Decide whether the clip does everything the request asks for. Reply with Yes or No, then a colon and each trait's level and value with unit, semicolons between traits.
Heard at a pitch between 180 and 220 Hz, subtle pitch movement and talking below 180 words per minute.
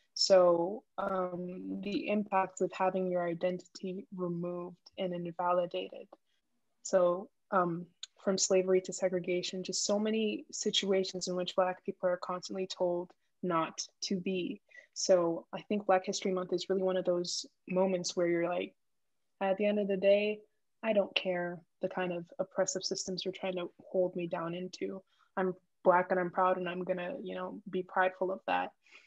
Yes: medium, 185 Hz; narrow, 1.2 semitones; average, 170 wpm